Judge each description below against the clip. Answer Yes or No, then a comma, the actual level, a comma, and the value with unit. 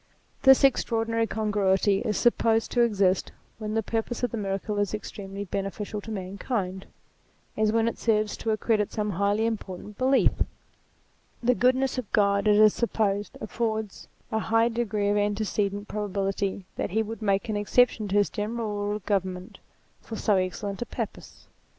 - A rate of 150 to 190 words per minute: Yes, average, 165 wpm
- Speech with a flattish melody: Yes, narrow, 2.1 semitones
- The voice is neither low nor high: No, high, 210 Hz